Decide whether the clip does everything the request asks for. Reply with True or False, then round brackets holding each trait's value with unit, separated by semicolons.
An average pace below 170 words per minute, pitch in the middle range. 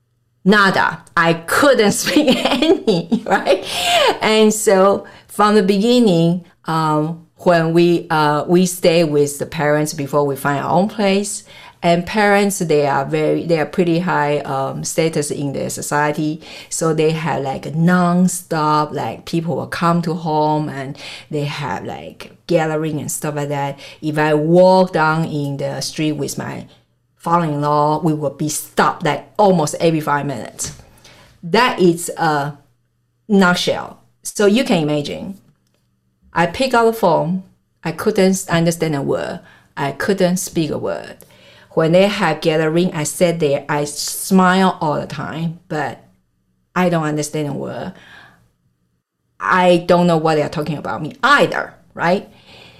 True (150 wpm; 160 Hz)